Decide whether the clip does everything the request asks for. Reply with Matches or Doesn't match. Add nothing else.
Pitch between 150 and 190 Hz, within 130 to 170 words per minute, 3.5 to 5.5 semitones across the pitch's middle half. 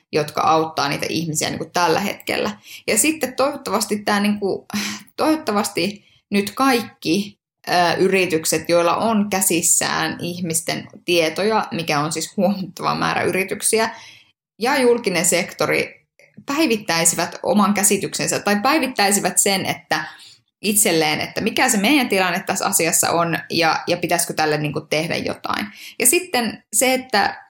Matches